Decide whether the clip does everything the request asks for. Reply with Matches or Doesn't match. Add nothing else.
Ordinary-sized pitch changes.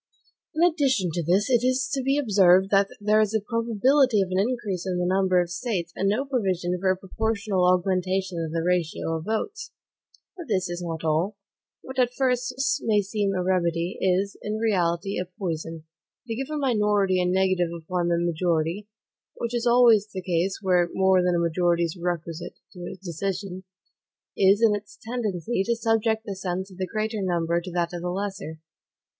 Matches